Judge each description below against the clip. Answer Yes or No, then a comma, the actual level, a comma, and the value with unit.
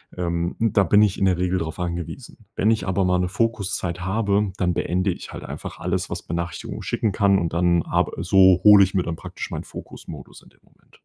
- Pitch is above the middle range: No, very low, 90 Hz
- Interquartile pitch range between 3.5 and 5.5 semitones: No, narrow, 2.5 semitones